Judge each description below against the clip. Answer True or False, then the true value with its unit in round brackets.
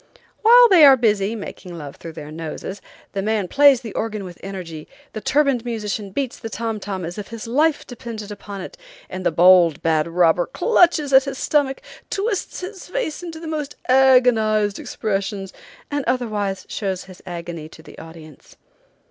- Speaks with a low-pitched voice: False (215 Hz)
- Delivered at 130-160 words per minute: False (175 wpm)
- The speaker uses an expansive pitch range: True (6.5 semitones)